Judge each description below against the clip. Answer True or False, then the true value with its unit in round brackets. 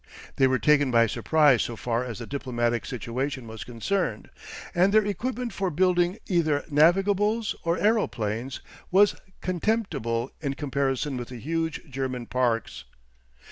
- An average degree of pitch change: False (6.9 semitones)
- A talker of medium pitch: True (145 Hz)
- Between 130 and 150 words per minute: True (140 wpm)